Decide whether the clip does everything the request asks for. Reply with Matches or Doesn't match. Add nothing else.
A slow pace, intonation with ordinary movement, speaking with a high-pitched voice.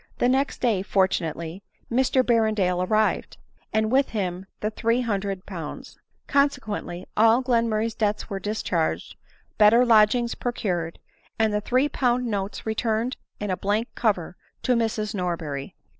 Matches